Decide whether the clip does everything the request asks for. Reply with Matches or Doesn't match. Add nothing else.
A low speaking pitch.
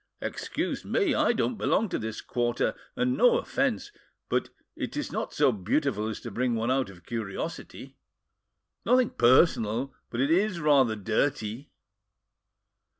Matches